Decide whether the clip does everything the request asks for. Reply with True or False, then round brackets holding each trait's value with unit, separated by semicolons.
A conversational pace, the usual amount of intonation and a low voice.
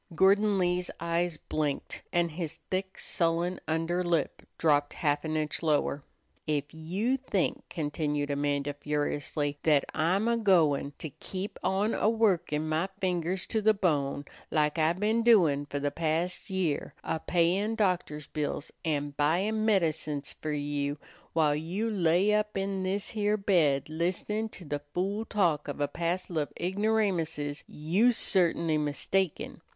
False (145 wpm; 4.4 semitones; 170 Hz)